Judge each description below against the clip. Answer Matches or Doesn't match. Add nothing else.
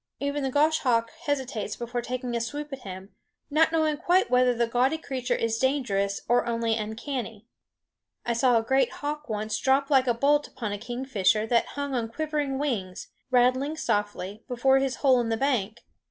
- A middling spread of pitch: Matches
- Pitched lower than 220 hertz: Doesn't match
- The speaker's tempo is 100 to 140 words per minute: Doesn't match